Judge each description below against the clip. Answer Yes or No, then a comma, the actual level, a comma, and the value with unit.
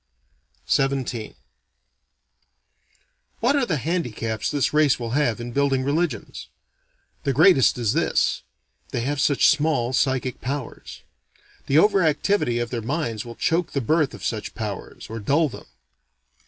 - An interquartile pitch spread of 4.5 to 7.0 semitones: Yes, average, 4.8 semitones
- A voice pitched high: No, low, 135 Hz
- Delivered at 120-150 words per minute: Yes, average, 140 wpm